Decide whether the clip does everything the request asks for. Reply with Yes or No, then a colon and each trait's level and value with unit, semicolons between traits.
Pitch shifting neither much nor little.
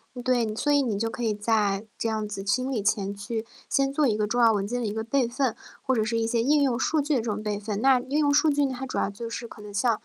Yes: average, 3.7 semitones